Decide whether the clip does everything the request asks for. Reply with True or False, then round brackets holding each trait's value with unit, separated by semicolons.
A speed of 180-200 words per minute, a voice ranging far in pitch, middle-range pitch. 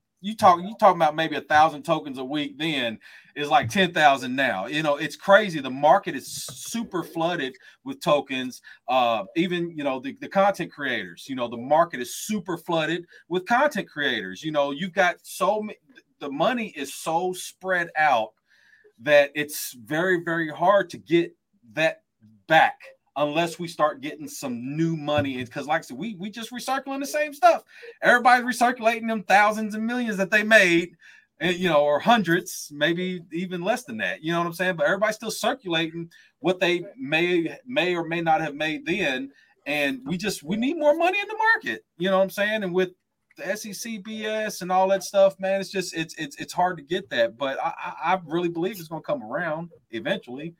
True (195 wpm; 5.7 semitones; 180 Hz)